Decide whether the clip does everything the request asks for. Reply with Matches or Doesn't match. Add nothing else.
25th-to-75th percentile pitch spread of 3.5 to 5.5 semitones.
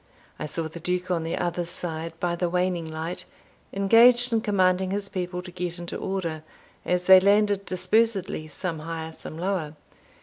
Doesn't match